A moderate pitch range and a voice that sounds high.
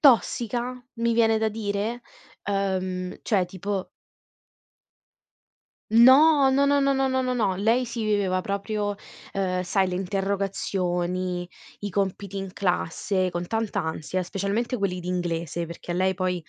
Yes: average, 3.7 semitones; high, 200 Hz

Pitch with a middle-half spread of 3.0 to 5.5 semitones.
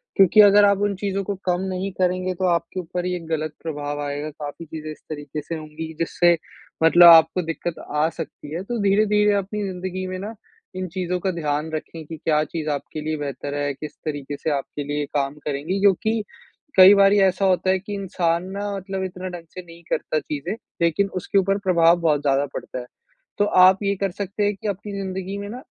Yes: average, 4.0 semitones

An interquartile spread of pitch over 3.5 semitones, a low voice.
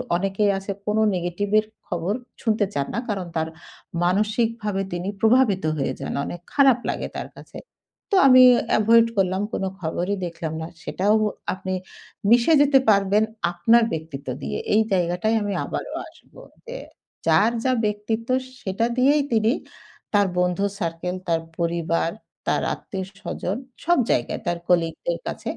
No: average, 4.2 semitones; high, 200 Hz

